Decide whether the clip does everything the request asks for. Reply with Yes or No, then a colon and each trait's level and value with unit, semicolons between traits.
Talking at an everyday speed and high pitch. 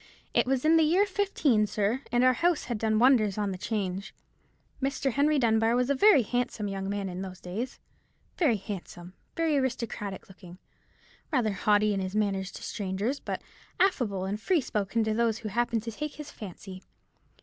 Yes: average, 175 wpm; high, 220 Hz